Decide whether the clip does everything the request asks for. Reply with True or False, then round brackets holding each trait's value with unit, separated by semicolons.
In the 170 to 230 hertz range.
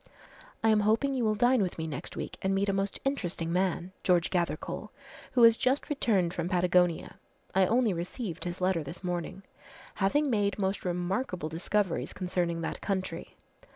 True (190 Hz)